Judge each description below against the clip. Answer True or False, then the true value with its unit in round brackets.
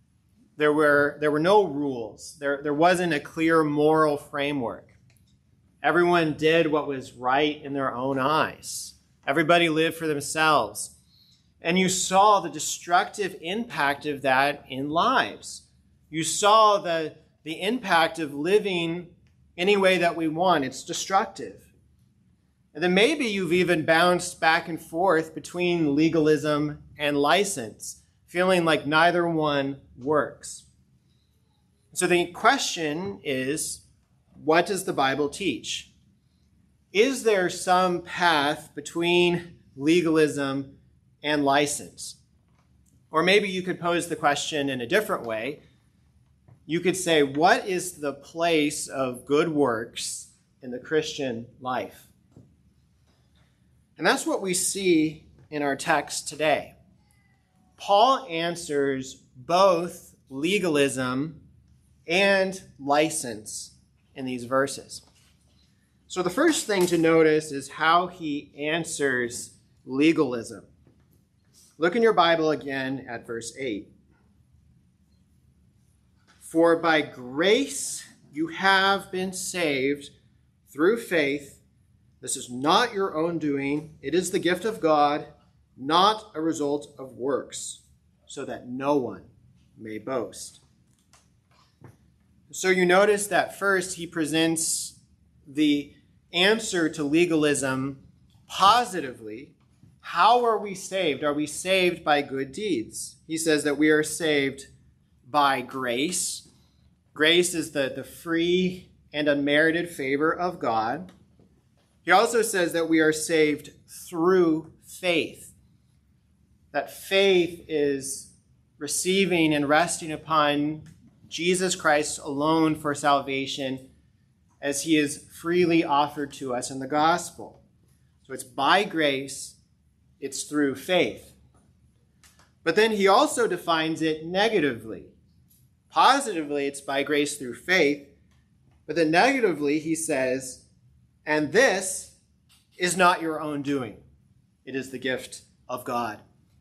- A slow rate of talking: True (120 wpm)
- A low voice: False (155 Hz)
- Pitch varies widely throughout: False (3.8 semitones)